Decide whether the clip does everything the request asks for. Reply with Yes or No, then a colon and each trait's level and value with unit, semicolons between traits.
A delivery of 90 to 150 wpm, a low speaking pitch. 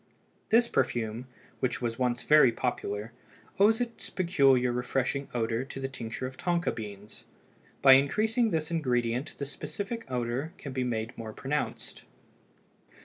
Yes: average, 140 wpm; low, 130 Hz